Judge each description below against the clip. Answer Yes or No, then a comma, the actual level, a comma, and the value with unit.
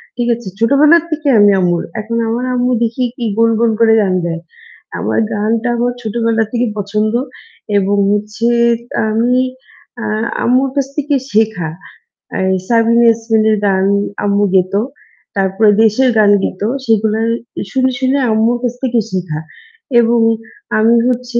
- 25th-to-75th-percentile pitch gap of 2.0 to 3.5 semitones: Yes, narrow, 2.6 semitones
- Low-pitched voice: No, high, 225 Hz